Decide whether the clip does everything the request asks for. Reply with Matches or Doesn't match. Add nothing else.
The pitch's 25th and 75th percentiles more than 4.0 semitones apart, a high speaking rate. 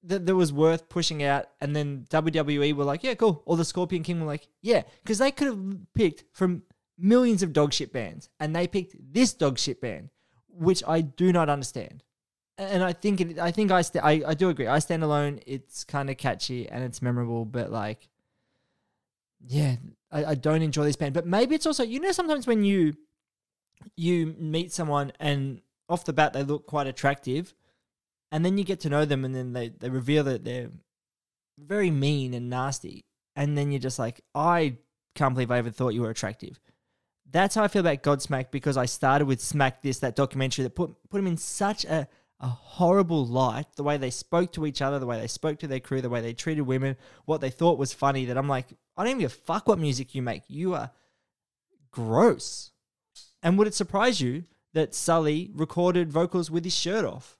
Matches